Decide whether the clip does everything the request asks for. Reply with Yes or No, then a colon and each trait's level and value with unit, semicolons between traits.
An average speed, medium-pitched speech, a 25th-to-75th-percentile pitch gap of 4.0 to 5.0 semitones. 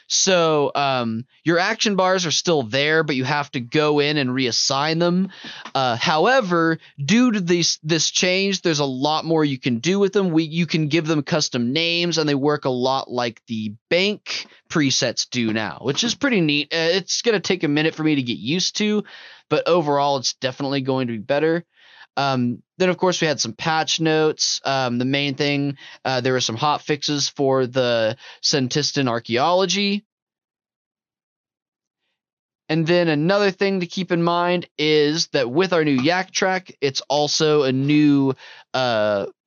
Yes: average, 180 wpm; medium, 150 Hz; average, 4.4 semitones